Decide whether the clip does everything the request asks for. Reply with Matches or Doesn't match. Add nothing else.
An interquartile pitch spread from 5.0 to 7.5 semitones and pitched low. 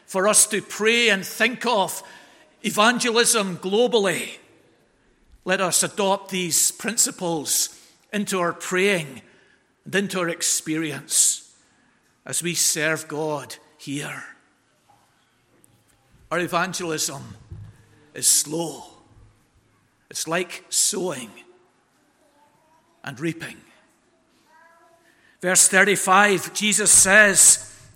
Doesn't match